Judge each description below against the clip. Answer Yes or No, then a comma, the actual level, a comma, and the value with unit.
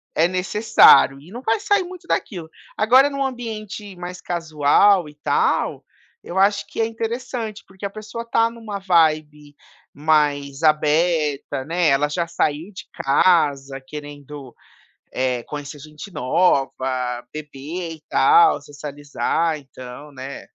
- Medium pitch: Yes, medium, 165 Hz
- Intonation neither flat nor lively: No, wide, 6.0 semitones